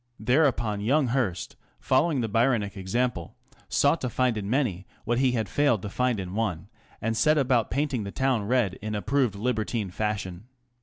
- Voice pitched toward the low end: Yes, low, 115 Hz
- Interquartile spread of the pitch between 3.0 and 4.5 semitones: Yes, average, 4.1 semitones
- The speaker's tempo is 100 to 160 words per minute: No, average, 170 wpm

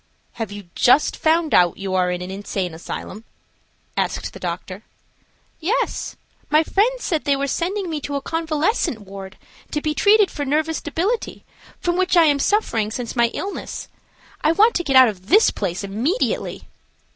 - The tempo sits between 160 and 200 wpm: Yes, average, 170 wpm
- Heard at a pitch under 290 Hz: No, very high, 295 Hz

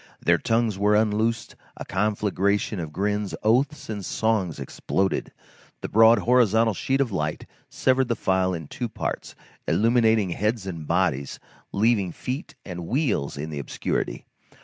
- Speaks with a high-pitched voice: No, low, 105 Hz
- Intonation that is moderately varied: Yes, average, 3.7 semitones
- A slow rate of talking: No, average, 145 wpm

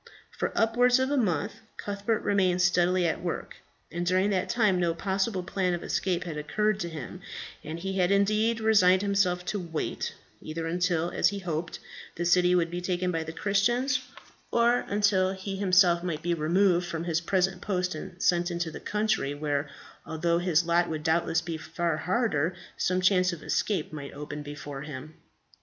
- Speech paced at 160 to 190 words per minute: Yes, average, 180 wpm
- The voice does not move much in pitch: No, average, 3.1 semitones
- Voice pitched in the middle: Yes, medium, 180 Hz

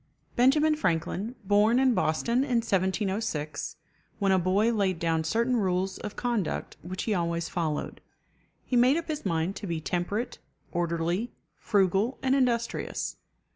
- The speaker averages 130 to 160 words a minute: Yes, average, 140 wpm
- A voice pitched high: Yes, high, 200 Hz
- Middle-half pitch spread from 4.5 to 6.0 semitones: Yes, wide, 5.4 semitones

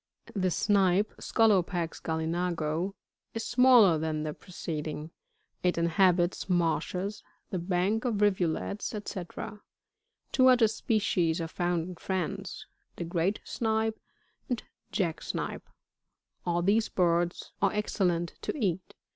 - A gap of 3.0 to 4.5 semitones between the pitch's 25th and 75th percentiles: Yes, average, 3.6 semitones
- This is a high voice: No, medium, 180 Hz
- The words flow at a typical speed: No, slow, 130 wpm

